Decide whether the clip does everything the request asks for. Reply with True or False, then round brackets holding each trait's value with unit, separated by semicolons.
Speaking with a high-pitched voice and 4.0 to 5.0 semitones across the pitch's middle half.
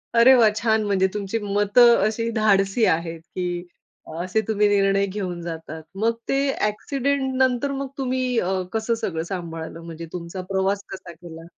True (200 Hz; 4.7 semitones)